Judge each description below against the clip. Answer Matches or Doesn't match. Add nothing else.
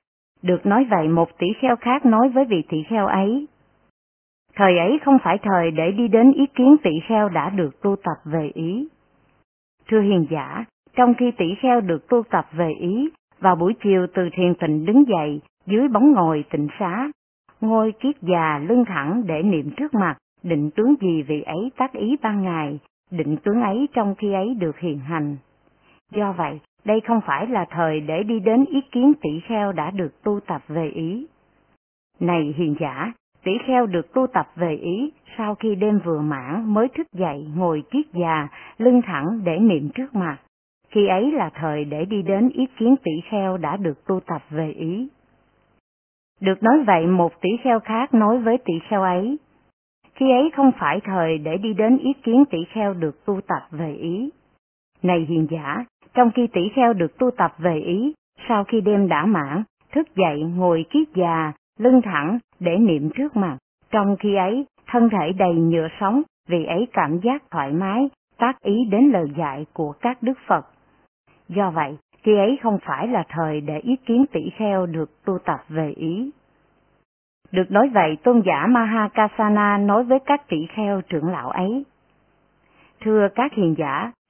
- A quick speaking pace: Doesn't match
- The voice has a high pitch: Matches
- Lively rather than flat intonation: Matches